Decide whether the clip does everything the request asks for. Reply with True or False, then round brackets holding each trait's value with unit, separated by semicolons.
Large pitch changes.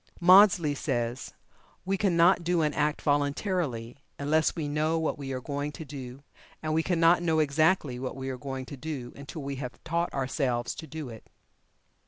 False (3.6 semitones)